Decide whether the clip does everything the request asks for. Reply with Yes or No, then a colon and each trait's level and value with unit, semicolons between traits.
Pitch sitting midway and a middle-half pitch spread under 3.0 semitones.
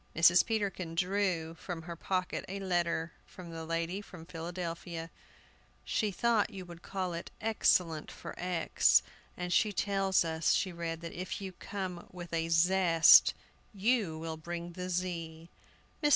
Yes: medium, 175 Hz; narrow, 2.4 semitones